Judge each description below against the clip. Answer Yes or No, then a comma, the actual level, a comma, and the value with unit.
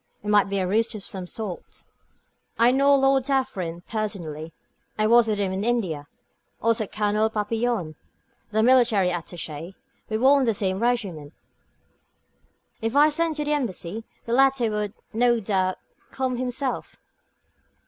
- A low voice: No, high, 220 Hz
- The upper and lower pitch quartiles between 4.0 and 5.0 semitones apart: Yes, average, 4.5 semitones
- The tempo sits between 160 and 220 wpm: No, average, 150 wpm